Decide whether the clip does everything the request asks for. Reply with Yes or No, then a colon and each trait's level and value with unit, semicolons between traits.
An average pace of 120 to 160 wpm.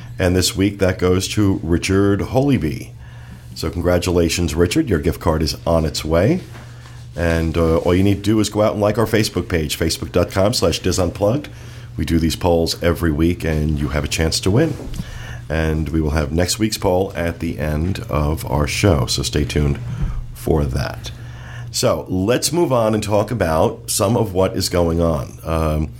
No: average, 185 wpm